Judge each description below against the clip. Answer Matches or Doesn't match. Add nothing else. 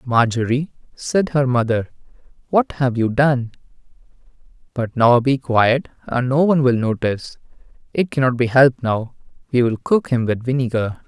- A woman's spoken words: Doesn't match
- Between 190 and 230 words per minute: Doesn't match